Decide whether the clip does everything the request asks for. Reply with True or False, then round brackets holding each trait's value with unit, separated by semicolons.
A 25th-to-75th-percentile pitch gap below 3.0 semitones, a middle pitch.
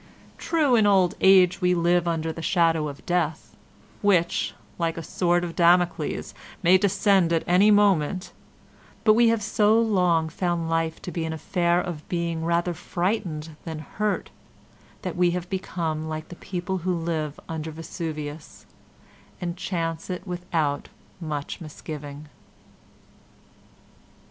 True (2.4 semitones; 175 Hz)